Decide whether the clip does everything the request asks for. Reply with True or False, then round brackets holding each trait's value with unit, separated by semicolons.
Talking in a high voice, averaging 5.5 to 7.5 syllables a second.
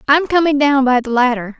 True (270 Hz; 5.6 syllables/s)